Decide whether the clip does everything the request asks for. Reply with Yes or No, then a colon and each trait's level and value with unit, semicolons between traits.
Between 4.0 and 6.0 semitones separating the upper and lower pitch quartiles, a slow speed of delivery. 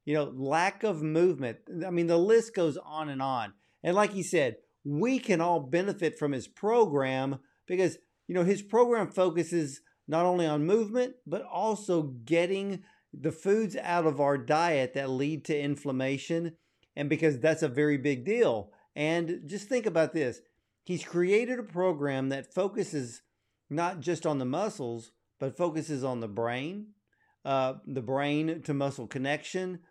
No: average, 4.7 semitones; average, 165 wpm